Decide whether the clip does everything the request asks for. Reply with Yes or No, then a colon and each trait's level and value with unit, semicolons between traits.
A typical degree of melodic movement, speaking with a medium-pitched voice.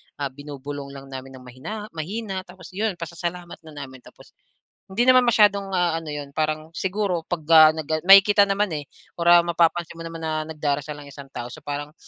Yes: average, 4.4 semitones; medium, 160 Hz